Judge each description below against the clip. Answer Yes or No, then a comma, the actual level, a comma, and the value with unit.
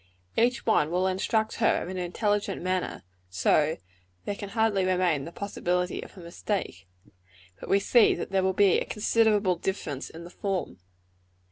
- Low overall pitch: No, high, 190 Hz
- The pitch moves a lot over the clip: No, average, 2.8 semitones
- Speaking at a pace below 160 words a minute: No, average, 170 wpm